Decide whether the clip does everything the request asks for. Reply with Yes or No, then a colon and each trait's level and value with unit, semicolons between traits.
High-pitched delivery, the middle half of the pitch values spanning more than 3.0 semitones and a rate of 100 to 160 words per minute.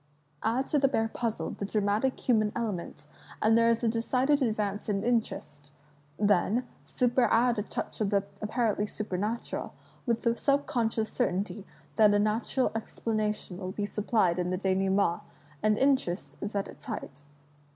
No: high, 215 Hz; narrow, 2.6 semitones; average, 155 wpm